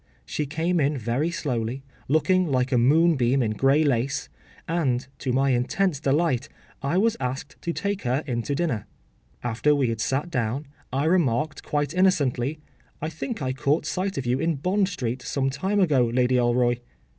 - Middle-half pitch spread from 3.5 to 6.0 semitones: Yes, average, 4.6 semitones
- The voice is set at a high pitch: No, medium, 140 Hz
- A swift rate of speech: No, average, 175 wpm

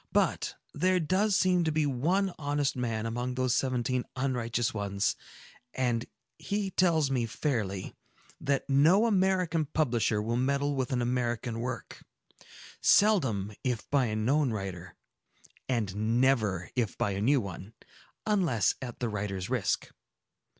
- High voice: No, low, 125 Hz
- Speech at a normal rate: No, slow, 130 wpm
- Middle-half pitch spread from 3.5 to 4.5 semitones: No, average, 5.1 semitones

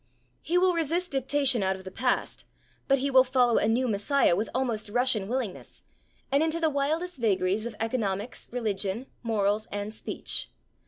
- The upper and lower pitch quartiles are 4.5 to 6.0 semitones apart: Yes, average, 5.0 semitones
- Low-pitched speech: No, high, 245 Hz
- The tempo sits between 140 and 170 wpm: Yes, average, 165 wpm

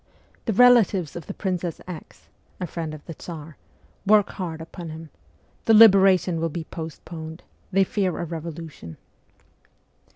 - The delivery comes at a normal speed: Yes, average, 155 wpm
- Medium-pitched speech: Yes, medium, 170 Hz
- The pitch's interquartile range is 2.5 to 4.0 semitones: Yes, average, 3.1 semitones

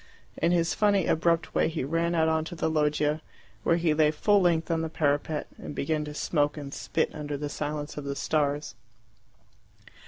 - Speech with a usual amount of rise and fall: No, narrow, 2.0 semitones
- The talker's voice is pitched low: No, medium, 155 Hz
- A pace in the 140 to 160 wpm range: No, average, 190 wpm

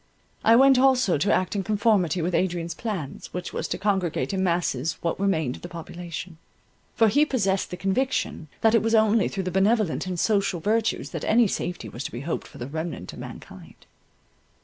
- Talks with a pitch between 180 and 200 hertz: Yes, high, 190 Hz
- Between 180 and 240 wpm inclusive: Yes, average, 195 wpm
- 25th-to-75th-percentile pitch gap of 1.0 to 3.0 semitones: No, average, 4.4 semitones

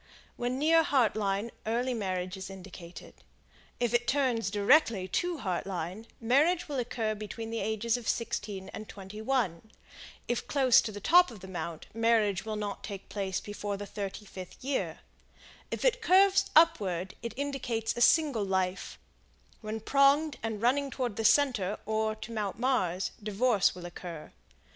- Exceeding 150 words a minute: Yes, average, 160 wpm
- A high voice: Yes, high, 220 Hz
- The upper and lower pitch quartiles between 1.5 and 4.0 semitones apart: No, average, 4.5 semitones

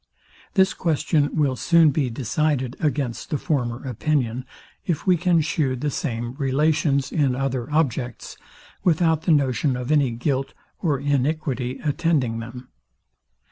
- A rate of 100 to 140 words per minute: Yes, slow, 135 wpm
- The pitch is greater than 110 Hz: Yes, medium, 140 Hz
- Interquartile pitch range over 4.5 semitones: No, average, 3.6 semitones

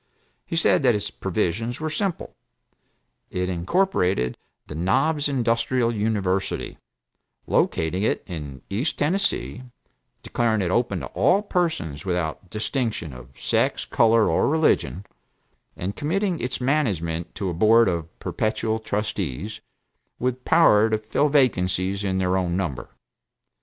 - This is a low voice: Yes, low, 105 Hz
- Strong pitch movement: Yes, wide, 6.0 semitones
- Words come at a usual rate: No, slow, 125 wpm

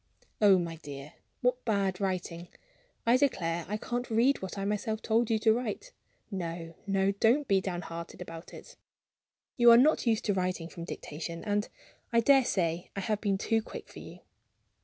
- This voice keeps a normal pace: Yes, average, 175 wpm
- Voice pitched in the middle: No, high, 200 Hz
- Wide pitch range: No, average, 4.9 semitones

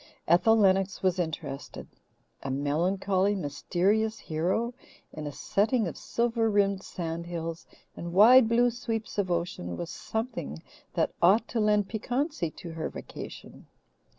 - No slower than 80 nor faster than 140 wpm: Yes, slow, 135 wpm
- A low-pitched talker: No, high, 190 Hz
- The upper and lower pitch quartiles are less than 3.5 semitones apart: No, average, 4.9 semitones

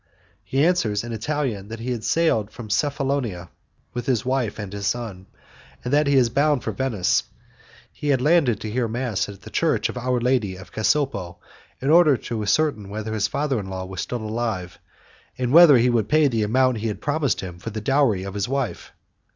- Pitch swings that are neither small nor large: Yes, average, 4.8 semitones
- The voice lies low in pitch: Yes, low, 120 Hz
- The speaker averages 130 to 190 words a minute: No, fast, 205 wpm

